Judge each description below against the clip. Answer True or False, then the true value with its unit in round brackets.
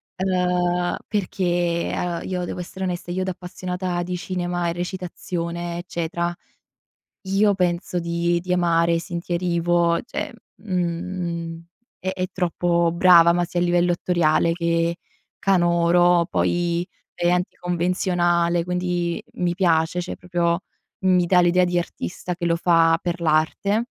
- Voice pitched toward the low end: False (175 Hz)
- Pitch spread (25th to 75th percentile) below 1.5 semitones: True (0.9 semitones)